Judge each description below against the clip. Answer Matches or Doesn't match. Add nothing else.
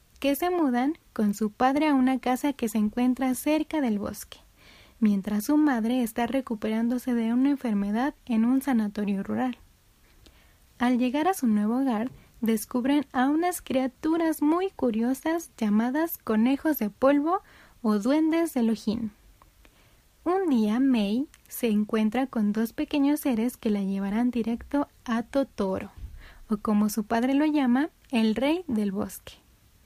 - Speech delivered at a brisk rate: Doesn't match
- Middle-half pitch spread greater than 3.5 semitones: Matches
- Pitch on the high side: Matches